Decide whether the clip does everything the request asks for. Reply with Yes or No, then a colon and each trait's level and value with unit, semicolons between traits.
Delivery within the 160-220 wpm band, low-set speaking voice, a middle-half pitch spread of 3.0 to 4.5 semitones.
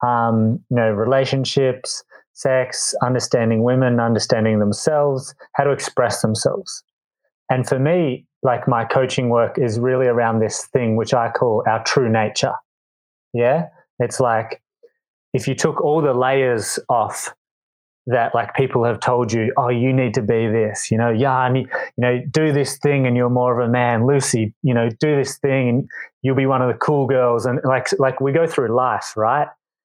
No: average, 185 wpm; low, 125 Hz; narrow, 2.5 semitones